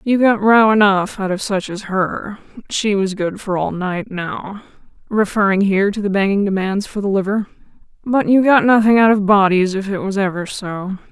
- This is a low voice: No, high, 200 Hz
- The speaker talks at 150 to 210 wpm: Yes, average, 195 wpm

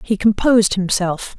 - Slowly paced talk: Yes, slow, 130 wpm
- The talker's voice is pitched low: No, high, 200 Hz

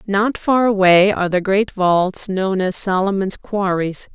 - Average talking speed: Yes, average, 160 wpm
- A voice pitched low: No, high, 195 Hz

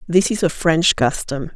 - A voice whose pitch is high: No, medium, 165 Hz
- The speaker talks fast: No, average, 195 wpm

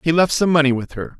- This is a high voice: No, medium, 145 Hz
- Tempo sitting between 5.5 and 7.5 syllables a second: Yes, 6.4 syllables/s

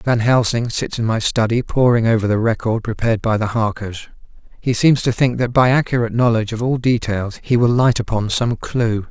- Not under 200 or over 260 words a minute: Yes, fast, 205 wpm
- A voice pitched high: No, low, 115 Hz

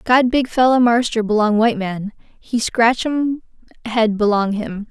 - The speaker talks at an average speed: Yes, average, 160 wpm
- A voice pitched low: No, high, 230 Hz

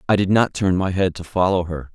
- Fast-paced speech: Yes, fast, 280 wpm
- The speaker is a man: Yes, male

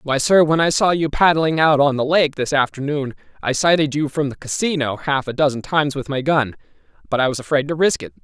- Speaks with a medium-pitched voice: Yes, medium, 145 Hz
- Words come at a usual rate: No, fast, 240 wpm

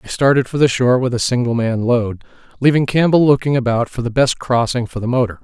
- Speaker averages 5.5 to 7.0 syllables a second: Yes, 6.1 syllables/s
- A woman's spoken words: No, male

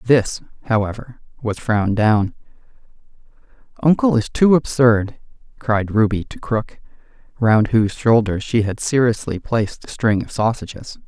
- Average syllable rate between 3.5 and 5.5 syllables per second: Yes, 4.6 syllables/s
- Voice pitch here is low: Yes, low, 115 Hz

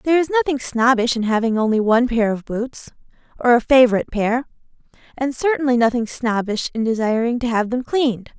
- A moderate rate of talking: Yes, average, 180 wpm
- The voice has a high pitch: Yes, high, 240 Hz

